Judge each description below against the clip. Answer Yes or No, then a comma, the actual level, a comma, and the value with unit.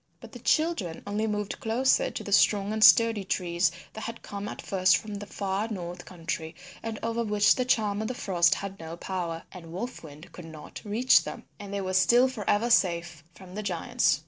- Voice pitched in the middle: No, high, 200 Hz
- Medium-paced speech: No, fast, 210 wpm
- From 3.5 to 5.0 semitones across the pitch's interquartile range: Yes, average, 4.0 semitones